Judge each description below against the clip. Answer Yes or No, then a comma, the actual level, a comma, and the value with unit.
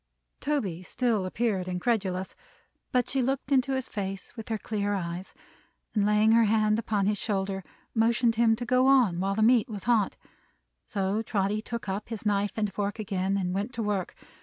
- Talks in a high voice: Yes, high, 210 Hz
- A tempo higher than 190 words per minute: No, average, 185 wpm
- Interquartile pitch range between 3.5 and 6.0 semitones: No, average, 3.1 semitones